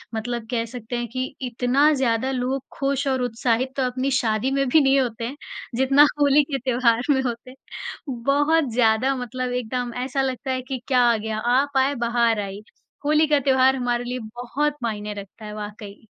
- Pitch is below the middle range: No, very high, 250 Hz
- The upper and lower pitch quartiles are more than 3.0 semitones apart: No, narrow, 2.5 semitones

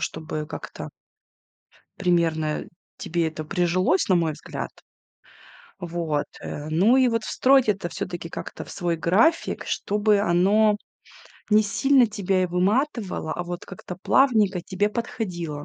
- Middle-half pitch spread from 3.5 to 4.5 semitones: Yes, average, 3.9 semitones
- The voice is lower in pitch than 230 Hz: Yes, medium, 185 Hz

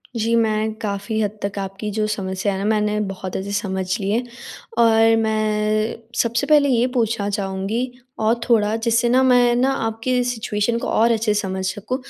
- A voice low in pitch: No, high, 220 Hz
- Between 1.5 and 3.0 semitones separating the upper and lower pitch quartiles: Yes, narrow, 2.4 semitones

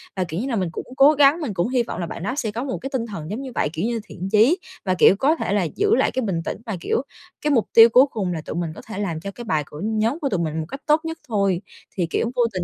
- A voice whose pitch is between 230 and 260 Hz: No, high, 215 Hz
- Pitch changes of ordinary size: No, wide, 6.4 semitones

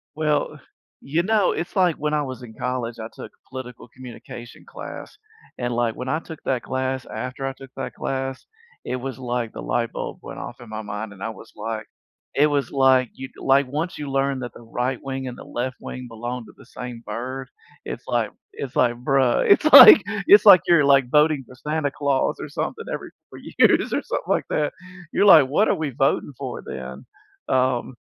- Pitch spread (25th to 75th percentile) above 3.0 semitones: No, average, 2.7 semitones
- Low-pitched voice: Yes, low, 130 Hz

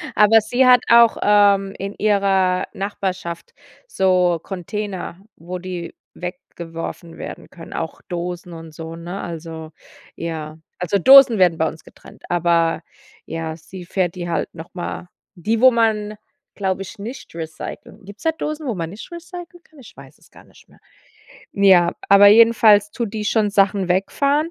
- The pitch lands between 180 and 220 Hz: Yes, high, 190 Hz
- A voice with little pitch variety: No, average, 3.8 semitones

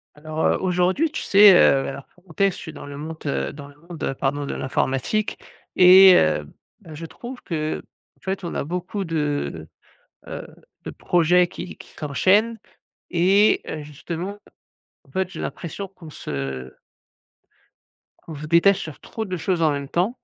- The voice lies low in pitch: No, medium, 170 Hz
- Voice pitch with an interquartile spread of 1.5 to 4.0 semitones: No, average, 4.5 semitones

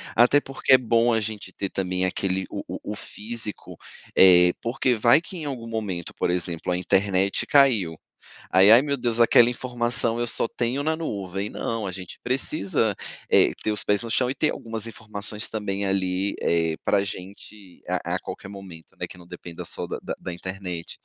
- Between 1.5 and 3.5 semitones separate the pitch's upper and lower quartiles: No, average, 4.1 semitones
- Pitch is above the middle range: No, low, 105 Hz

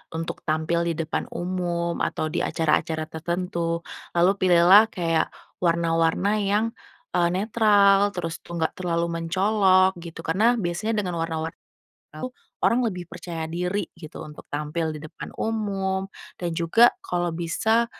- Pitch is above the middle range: No, medium, 175 Hz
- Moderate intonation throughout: Yes, average, 3.1 semitones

